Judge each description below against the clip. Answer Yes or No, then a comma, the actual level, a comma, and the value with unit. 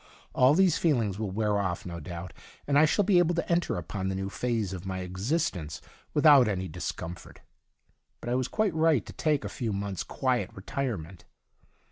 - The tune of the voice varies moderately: No, wide, 7.9 semitones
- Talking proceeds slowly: No, average, 195 wpm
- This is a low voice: Yes, low, 110 Hz